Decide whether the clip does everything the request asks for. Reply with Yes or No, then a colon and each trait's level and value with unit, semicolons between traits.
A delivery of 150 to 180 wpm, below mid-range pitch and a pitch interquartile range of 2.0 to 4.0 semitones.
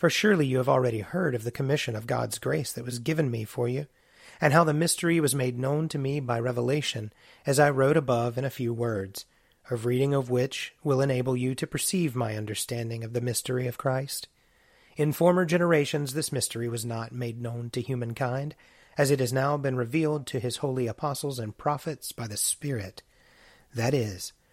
No: average, 200 wpm; low, 130 Hz; average, 3.6 semitones